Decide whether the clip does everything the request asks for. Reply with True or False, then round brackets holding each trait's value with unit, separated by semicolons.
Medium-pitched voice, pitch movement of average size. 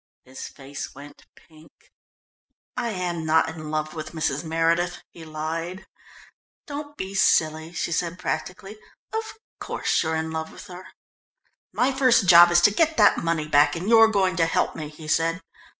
True (165 Hz; 3.2 semitones)